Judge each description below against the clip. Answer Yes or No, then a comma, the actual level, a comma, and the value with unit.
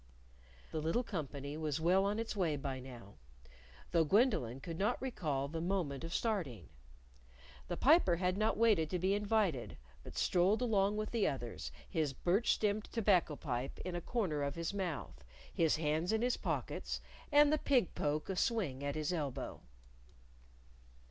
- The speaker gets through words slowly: No, average, 165 wpm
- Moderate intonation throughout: No, wide, 6.3 semitones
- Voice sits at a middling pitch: Yes, medium, 175 Hz